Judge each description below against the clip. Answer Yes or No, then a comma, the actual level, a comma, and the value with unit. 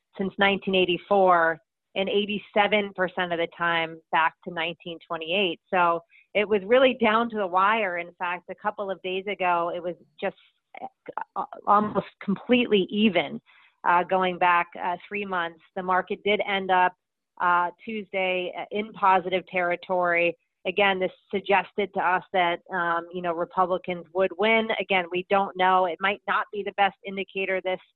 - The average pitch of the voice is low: No, medium, 185 Hz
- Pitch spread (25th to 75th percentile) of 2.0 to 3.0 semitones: Yes, narrow, 2.4 semitones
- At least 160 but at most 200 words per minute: No, average, 150 wpm